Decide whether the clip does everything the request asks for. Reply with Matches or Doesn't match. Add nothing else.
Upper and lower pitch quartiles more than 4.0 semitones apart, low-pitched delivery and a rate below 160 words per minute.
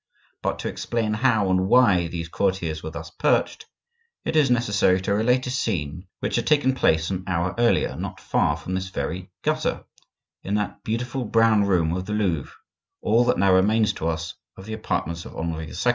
Doesn't match